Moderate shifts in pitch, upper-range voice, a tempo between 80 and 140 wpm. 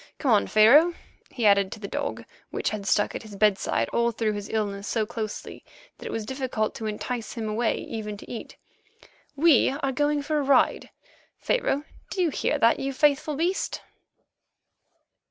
No: average, 4.9 semitones; high, 235 Hz; average, 175 wpm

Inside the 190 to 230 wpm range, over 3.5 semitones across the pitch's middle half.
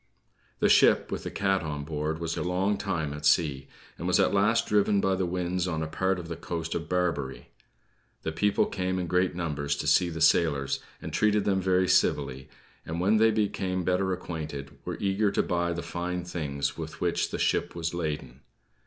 No: average, 200 wpm; average, 3.2 semitones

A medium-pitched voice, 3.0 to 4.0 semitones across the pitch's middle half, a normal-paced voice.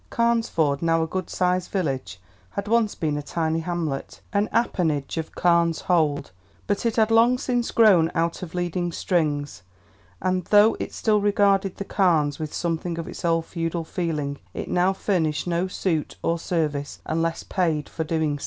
Yes: medium, 170 Hz; average, 3.4 semitones; average, 170 wpm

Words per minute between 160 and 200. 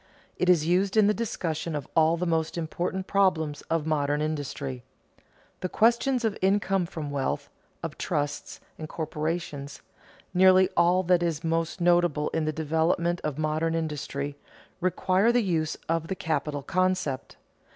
No: average, 150 wpm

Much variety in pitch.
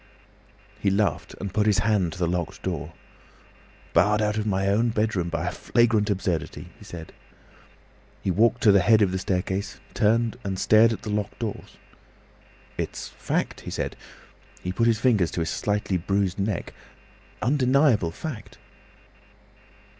No: average, 2.9 semitones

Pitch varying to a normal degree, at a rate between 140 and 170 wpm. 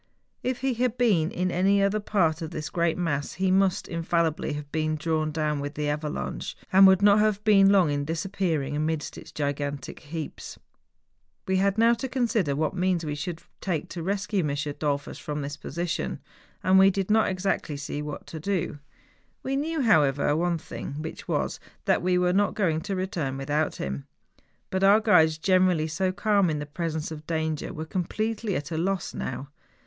No: average, 4.3 semitones; average, 190 wpm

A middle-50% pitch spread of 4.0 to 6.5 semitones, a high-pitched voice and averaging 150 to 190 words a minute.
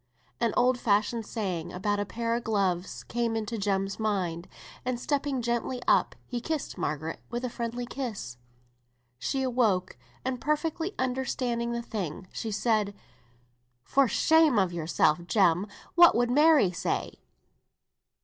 No: average, 4.4 semitones; high, 230 Hz; average, 140 wpm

